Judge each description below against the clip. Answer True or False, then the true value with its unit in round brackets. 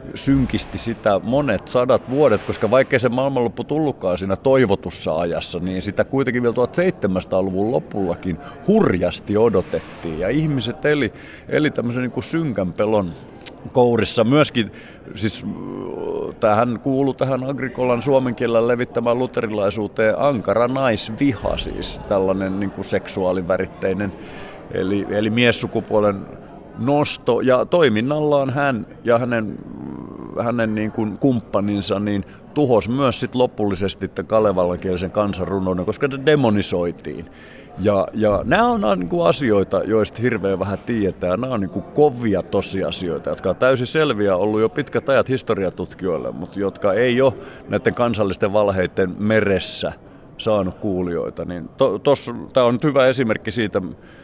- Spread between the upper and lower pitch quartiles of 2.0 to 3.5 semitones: False (4.8 semitones)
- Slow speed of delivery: False (125 wpm)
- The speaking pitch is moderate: False (110 Hz)